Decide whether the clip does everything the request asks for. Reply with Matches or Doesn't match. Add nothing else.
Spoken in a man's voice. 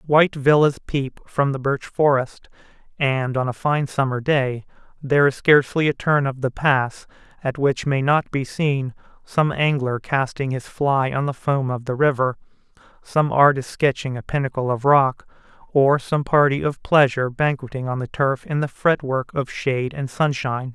Matches